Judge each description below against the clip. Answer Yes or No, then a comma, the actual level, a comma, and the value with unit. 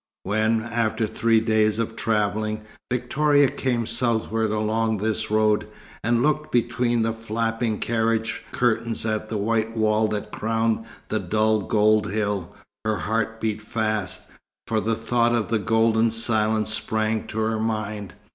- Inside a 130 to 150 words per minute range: Yes, average, 145 wpm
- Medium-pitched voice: No, low, 110 Hz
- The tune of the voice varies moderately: No, narrow, 0.9 semitones